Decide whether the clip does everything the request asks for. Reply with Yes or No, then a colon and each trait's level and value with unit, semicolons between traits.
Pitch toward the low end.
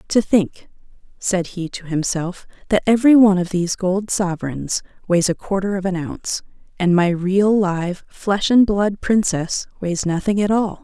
No: high, 190 Hz